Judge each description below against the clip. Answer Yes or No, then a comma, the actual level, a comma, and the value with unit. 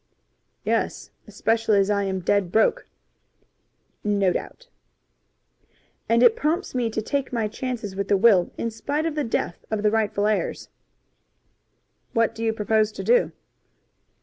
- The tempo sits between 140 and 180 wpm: Yes, average, 150 wpm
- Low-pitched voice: No, high, 220 Hz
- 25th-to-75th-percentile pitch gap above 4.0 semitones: No, average, 3.4 semitones